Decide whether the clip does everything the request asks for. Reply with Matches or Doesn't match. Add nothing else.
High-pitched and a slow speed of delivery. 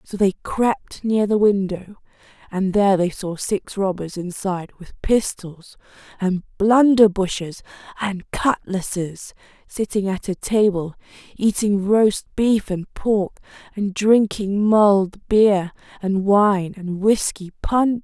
Matches